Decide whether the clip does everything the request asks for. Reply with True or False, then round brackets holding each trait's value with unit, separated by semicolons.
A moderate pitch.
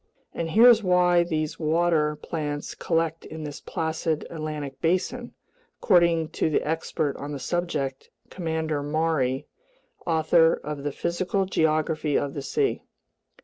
True (160 Hz)